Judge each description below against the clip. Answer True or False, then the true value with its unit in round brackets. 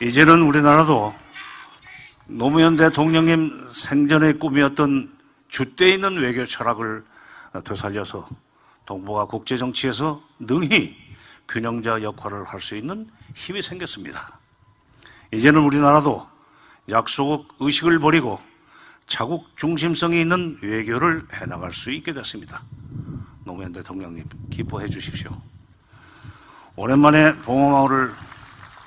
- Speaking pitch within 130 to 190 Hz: True (135 Hz)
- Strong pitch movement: True (5.8 semitones)